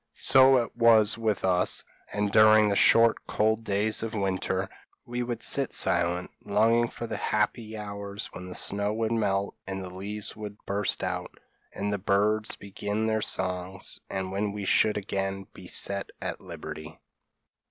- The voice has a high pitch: No, low, 105 Hz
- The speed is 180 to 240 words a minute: No, average, 165 wpm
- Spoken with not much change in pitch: Yes, narrow, 2.1 semitones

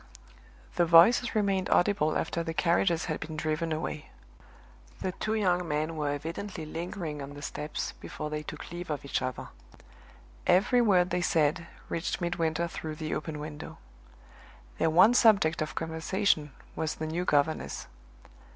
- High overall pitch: No, medium, 165 Hz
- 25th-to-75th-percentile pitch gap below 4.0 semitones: Yes, average, 2.8 semitones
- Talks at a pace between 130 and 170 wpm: Yes, average, 150 wpm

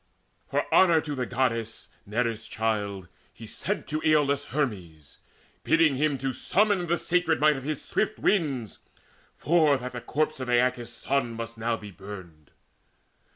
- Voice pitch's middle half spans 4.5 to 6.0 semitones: Yes, average, 5.3 semitones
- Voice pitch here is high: No, low, 130 Hz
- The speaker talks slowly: No, average, 150 wpm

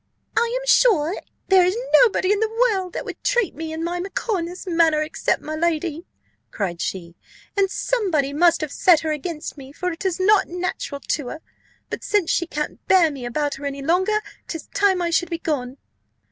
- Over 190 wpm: Yes, average, 200 wpm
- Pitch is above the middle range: Yes, very high, 340 Hz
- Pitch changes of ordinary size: Yes, average, 4.1 semitones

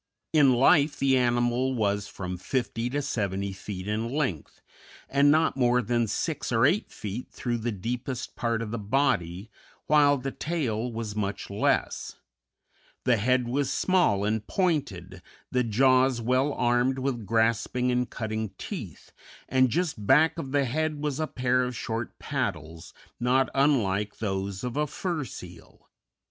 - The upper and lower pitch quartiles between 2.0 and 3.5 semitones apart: No, average, 4.1 semitones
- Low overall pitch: Yes, low, 125 Hz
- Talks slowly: No, average, 155 wpm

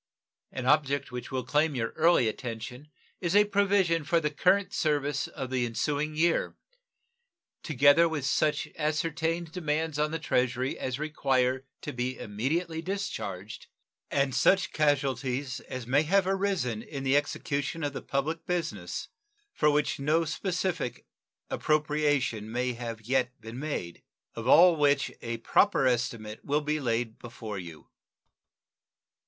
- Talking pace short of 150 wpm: Yes, average, 140 wpm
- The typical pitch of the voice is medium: Yes, medium, 145 Hz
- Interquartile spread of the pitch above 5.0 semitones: No, average, 4.4 semitones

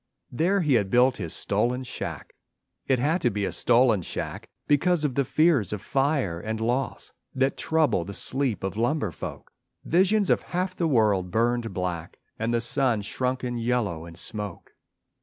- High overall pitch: No, low, 120 Hz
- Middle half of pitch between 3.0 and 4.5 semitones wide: No, average, 5.2 semitones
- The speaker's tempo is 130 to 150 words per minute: No, average, 170 wpm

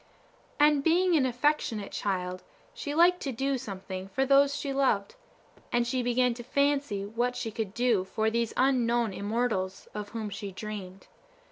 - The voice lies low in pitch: No, high, 235 Hz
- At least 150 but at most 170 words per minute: Yes, average, 160 wpm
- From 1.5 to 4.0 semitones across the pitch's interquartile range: No, average, 5.1 semitones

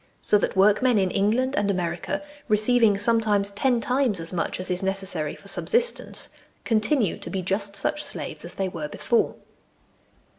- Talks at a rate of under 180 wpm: Yes, average, 160 wpm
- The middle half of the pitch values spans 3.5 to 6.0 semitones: Yes, average, 3.9 semitones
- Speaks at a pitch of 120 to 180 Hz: No, high, 205 Hz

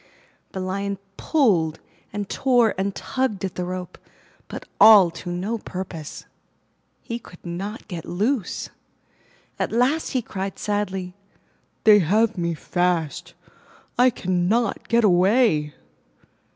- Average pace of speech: No, slow, 120 wpm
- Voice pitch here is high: Yes, high, 195 Hz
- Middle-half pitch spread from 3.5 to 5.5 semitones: Yes, average, 4.0 semitones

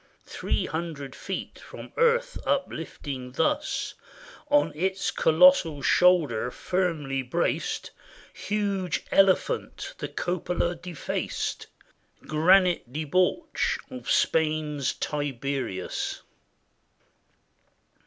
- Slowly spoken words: Yes, slow, 75 wpm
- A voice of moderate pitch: Yes, medium, 165 Hz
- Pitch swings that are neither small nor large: Yes, average, 4.7 semitones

